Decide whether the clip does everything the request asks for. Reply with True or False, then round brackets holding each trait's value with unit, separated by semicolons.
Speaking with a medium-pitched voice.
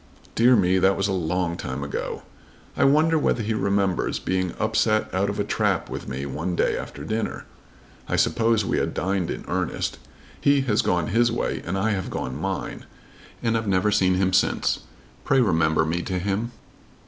False (95 Hz)